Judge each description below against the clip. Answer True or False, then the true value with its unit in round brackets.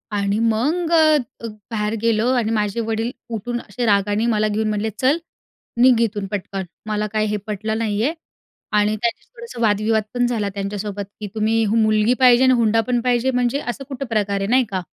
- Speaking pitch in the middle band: False (220 Hz)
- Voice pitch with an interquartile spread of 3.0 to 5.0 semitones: False (2.5 semitones)